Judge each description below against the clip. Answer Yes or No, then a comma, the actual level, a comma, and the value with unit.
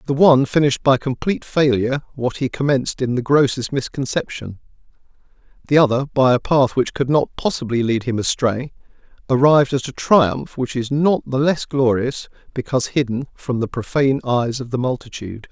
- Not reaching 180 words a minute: Yes, average, 170 wpm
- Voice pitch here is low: Yes, low, 130 Hz